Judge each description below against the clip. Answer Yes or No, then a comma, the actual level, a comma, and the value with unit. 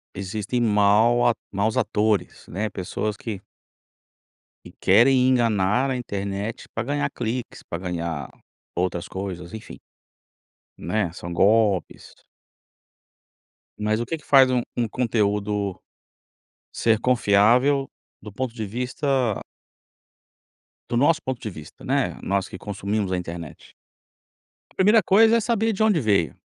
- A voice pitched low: Yes, low, 110 Hz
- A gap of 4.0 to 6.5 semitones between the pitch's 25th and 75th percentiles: Yes, average, 4.3 semitones